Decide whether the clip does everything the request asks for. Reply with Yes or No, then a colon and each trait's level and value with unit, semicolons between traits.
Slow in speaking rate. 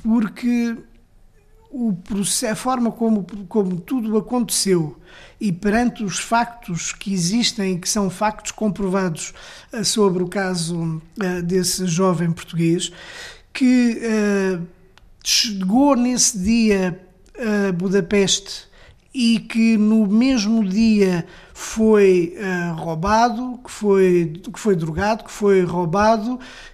Yes: slow, 105 wpm